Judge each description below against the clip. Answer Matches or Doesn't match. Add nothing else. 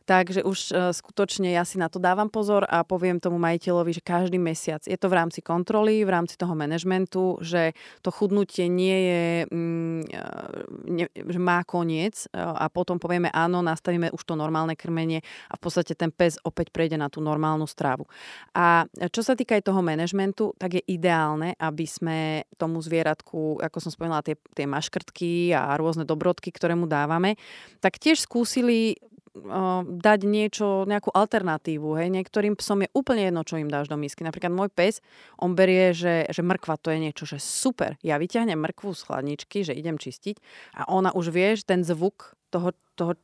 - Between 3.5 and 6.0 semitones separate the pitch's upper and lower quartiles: Doesn't match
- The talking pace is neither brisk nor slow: Doesn't match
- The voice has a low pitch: Doesn't match